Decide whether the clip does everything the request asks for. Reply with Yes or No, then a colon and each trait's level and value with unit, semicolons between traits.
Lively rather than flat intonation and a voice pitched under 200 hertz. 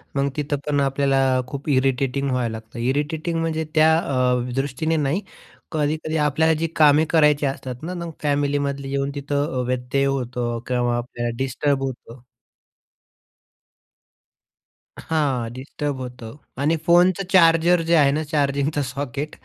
No: average, 3.3 semitones; medium, 140 Hz